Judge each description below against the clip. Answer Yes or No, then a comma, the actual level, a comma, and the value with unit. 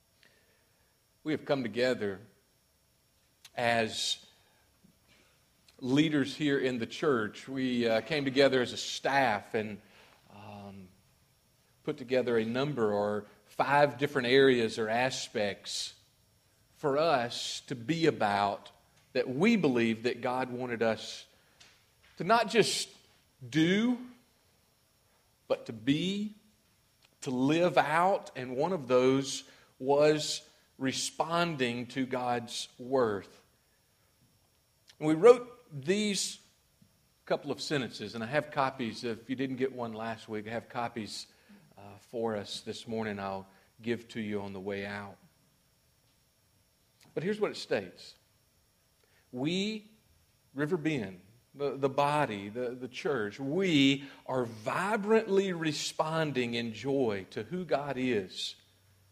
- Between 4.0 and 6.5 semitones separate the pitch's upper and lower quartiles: Yes, average, 4.7 semitones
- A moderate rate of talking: No, slow, 120 wpm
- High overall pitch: No, low, 125 Hz